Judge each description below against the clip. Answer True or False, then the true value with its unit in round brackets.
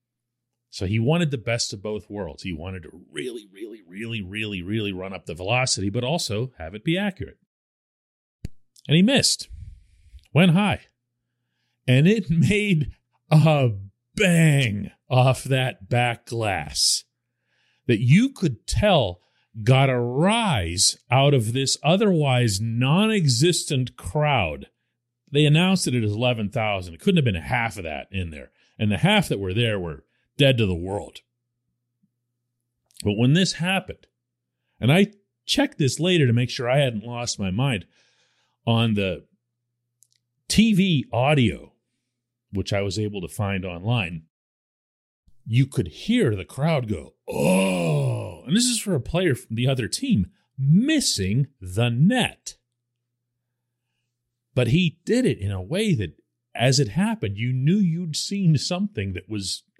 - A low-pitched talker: True (120 Hz)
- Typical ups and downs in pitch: False (6.4 semitones)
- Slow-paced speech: False (145 wpm)